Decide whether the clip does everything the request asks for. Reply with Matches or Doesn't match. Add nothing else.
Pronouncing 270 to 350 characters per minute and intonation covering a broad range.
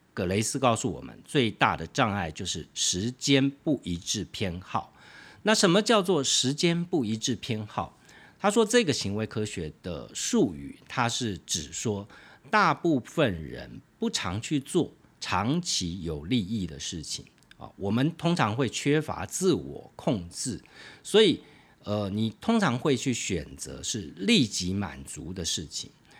Doesn't match